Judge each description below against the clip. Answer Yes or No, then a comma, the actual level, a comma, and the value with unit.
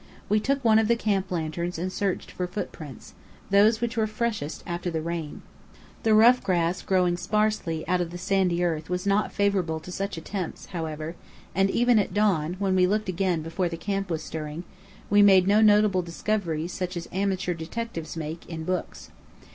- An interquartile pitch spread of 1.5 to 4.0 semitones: Yes, average, 3.5 semitones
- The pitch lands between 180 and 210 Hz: Yes, medium, 185 Hz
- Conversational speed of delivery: Yes, average, 185 wpm